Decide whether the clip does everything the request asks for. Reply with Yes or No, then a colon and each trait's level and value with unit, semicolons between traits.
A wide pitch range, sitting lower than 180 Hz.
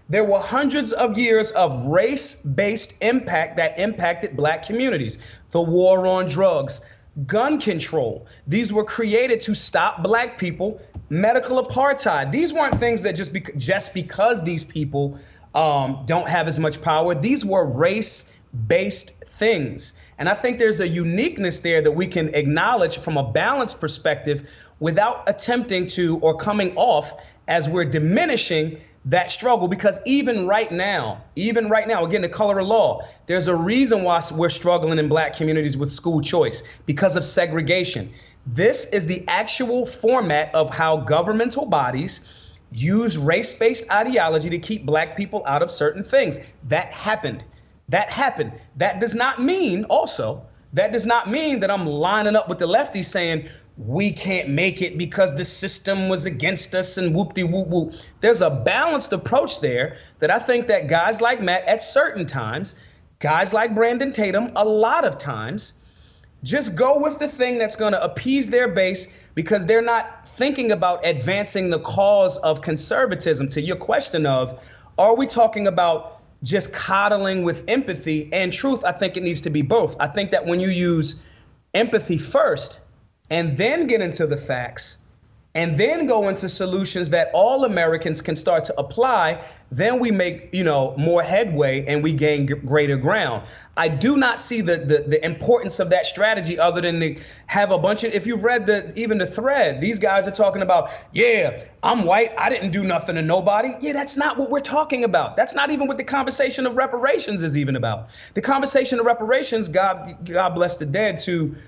No: wide, 6.0 semitones; medium, 185 Hz